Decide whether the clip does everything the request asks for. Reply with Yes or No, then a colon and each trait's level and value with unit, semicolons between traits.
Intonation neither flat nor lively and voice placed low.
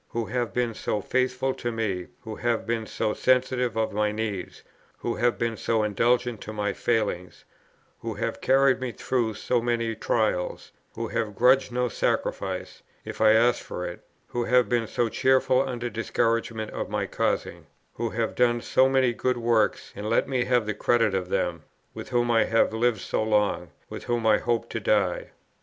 No: narrow, 2.2 semitones; low, 115 Hz